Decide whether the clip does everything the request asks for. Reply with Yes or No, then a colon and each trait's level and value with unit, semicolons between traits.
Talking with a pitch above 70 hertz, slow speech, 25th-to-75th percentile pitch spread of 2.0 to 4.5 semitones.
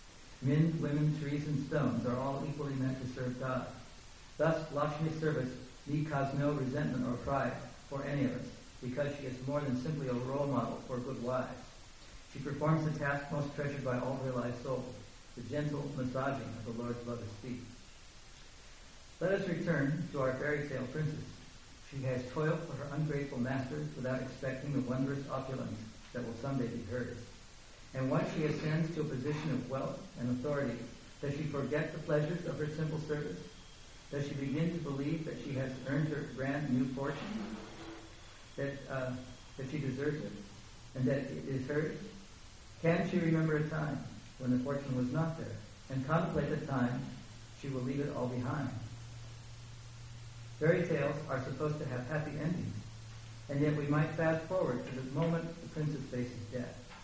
No: low, 135 Hz; average, 175 wpm; average, 3.2 semitones